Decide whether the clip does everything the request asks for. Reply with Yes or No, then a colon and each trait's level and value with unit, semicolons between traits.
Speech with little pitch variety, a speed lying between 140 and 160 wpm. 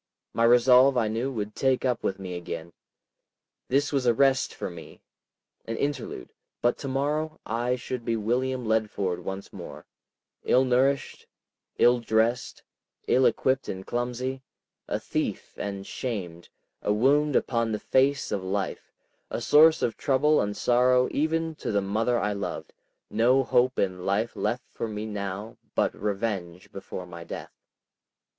No: average, 4.3 semitones; average, 150 wpm